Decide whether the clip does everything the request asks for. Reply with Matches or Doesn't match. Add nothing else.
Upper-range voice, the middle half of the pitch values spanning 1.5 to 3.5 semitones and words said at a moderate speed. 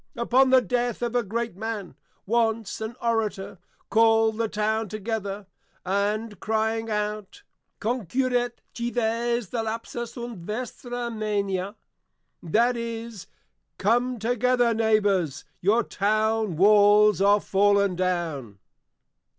Doesn't match